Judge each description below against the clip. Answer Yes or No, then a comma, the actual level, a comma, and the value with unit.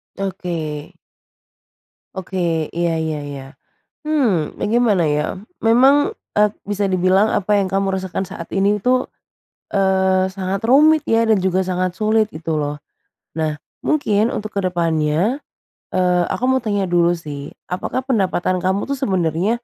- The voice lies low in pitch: No, high, 190 Hz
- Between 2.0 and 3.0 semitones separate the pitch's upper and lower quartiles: No, average, 4.0 semitones